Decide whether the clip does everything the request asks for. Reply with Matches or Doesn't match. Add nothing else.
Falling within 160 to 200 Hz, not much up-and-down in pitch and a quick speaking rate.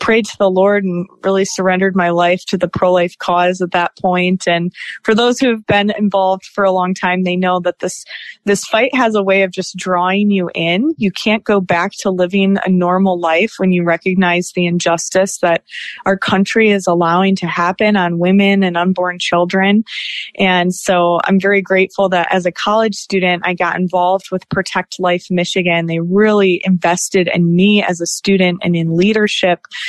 Doesn't match